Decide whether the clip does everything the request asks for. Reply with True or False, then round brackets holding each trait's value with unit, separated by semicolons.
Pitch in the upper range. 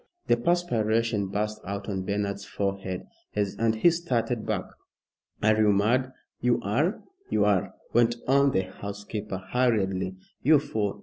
False (105 Hz)